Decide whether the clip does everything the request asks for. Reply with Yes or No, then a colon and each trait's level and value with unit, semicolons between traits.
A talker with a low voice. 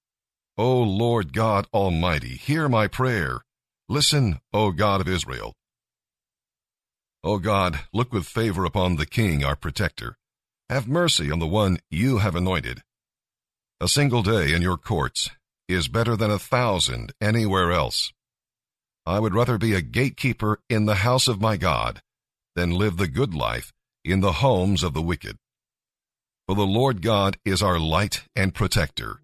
Yes: low, 105 Hz